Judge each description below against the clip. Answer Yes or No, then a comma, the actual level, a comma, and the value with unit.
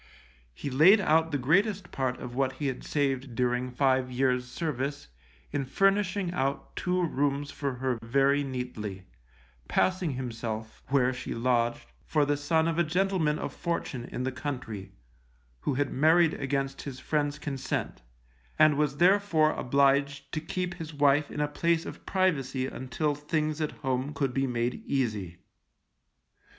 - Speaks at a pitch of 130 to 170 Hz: Yes, medium, 140 Hz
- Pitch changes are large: No, average, 3.4 semitones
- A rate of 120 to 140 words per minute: No, average, 155 wpm